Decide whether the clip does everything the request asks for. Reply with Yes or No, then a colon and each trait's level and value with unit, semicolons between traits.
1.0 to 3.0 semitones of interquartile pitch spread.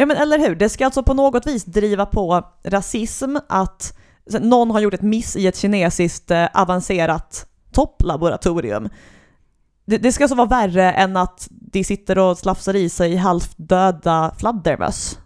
No: average, 3.8 semitones